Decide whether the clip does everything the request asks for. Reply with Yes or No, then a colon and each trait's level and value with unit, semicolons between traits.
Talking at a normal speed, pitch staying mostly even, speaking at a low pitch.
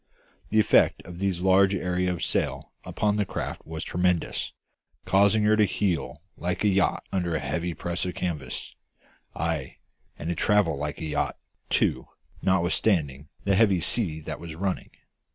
No: average, 160 wpm; average, 3.4 semitones; very low, 90 Hz